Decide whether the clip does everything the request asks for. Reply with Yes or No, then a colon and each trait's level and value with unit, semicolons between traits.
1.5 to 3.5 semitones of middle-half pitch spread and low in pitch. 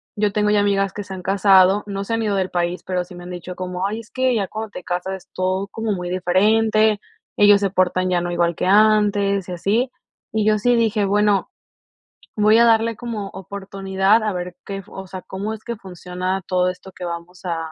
No: narrow, 2.6 semitones; high, 195 Hz